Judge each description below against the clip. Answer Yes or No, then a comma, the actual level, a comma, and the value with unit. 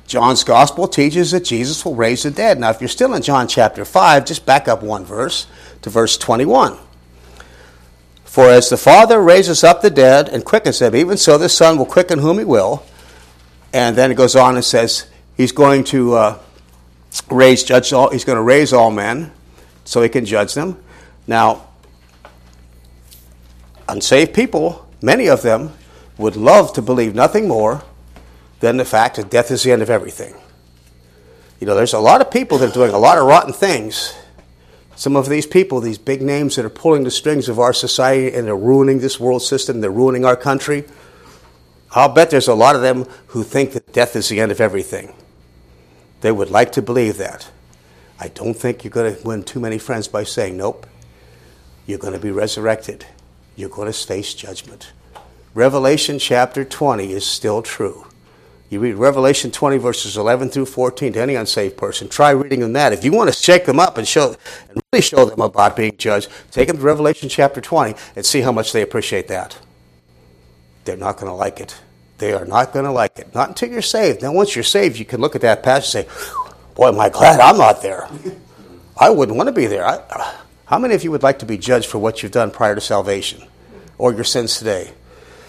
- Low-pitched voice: Yes, low, 120 Hz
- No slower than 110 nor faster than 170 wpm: No, fast, 205 wpm